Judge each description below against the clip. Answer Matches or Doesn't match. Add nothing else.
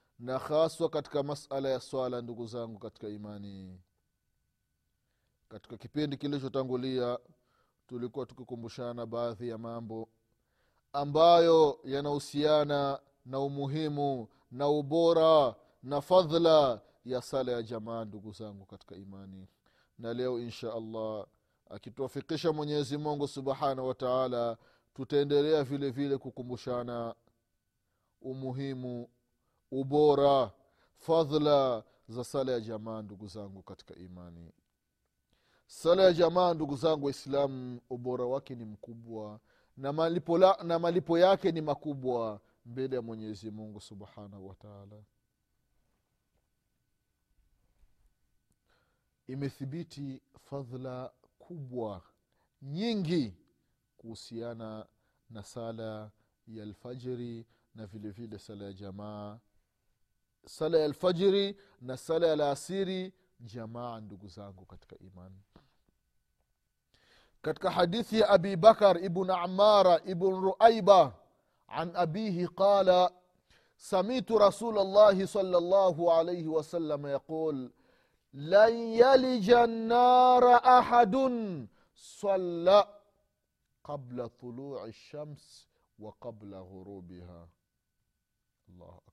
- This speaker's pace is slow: Matches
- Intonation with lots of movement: Matches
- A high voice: Doesn't match